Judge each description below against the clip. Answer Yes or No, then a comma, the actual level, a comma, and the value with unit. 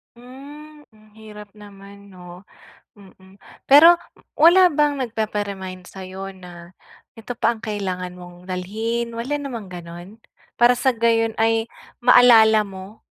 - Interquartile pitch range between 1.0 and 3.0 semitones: No, average, 4.1 semitones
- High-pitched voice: Yes, high, 215 Hz